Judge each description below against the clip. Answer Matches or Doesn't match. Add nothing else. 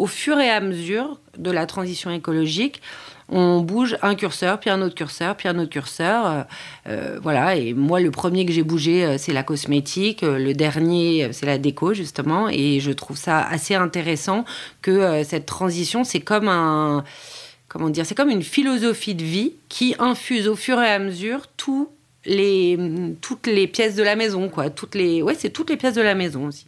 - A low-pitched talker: Doesn't match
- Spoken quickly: Doesn't match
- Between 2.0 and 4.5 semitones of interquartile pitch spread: Doesn't match